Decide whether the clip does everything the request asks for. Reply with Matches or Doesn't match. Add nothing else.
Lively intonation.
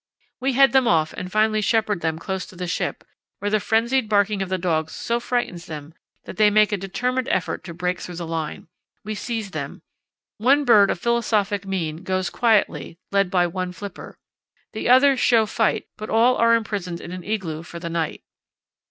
Doesn't match